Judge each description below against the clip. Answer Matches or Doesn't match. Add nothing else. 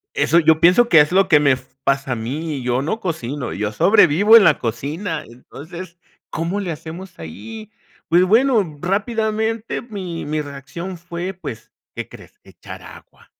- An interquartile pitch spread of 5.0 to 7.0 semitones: Matches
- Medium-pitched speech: Matches